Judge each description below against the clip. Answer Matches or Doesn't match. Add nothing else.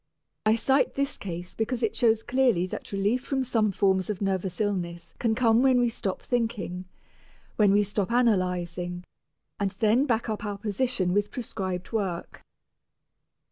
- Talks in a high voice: Matches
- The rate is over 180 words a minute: Doesn't match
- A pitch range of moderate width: Matches